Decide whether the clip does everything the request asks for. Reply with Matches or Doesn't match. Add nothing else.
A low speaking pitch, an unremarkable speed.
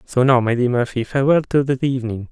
Doesn't match